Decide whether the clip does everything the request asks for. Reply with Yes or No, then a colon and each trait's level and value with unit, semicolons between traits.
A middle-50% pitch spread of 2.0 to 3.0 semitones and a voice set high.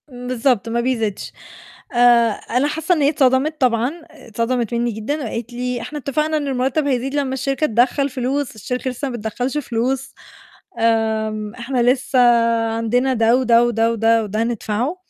Yes: average, 2.7 semitones; high, 245 Hz